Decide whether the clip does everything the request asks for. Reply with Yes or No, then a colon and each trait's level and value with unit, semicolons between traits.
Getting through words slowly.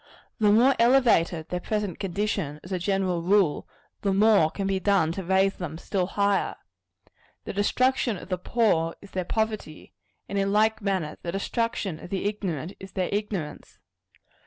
No: average, 165 wpm